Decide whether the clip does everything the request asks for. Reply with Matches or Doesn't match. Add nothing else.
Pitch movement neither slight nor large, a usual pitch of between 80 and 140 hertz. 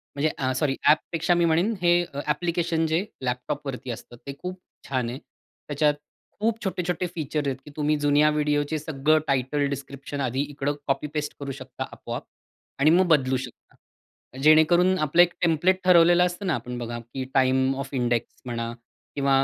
Doesn't match